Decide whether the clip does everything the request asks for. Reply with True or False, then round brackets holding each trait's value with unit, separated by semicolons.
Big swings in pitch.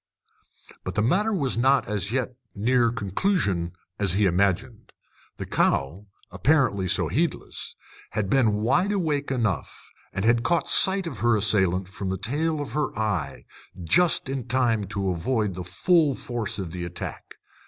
True (6.2 semitones)